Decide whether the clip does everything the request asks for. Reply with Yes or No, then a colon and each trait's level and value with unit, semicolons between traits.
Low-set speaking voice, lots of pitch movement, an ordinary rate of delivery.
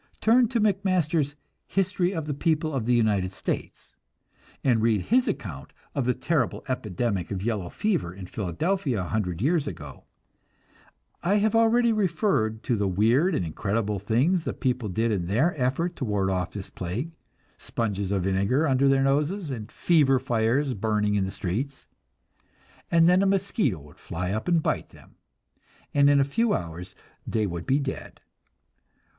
Yes: low, 125 Hz; wide, 8.6 semitones; average, 165 wpm